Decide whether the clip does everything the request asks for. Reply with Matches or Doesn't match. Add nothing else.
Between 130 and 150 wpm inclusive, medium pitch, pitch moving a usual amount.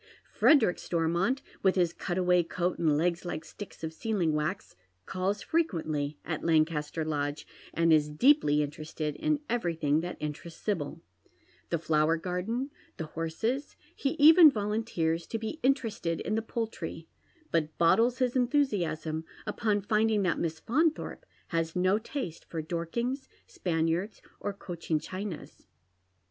Doesn't match